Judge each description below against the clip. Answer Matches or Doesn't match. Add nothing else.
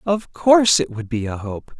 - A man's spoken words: Matches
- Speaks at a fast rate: Matches